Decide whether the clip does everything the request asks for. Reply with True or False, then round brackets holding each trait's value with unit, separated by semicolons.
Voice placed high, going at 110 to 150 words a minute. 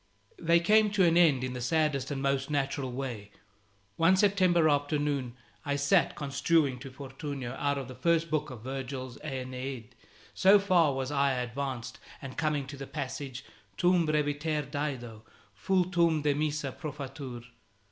False (140 Hz; 145 wpm)